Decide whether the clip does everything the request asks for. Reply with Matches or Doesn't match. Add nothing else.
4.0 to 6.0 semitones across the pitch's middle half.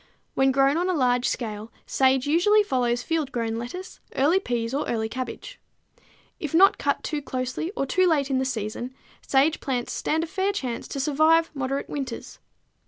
Matches